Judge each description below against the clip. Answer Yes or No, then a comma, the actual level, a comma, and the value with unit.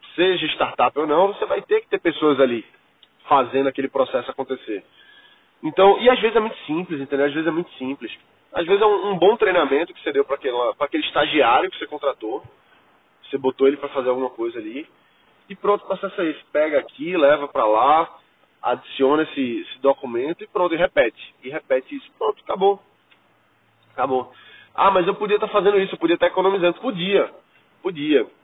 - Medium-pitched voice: No, high, 195 Hz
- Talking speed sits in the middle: No, fast, 195 wpm